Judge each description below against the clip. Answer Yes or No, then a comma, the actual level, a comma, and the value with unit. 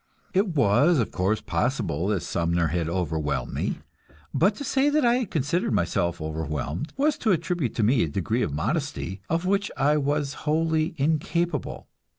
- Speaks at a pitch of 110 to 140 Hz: Yes, low, 135 Hz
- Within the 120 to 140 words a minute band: No, average, 165 wpm